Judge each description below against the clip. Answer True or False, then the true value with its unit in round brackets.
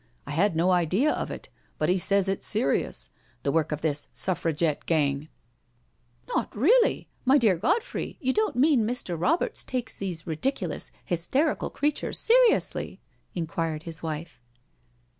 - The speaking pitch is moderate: True (180 Hz)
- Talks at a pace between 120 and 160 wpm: True (145 wpm)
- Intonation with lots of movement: True (8.5 semitones)